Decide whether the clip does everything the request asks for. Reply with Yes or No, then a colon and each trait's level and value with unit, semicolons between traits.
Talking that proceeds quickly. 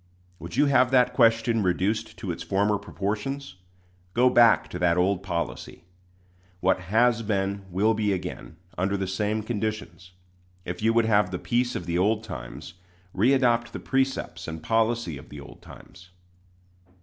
No: average, 160 wpm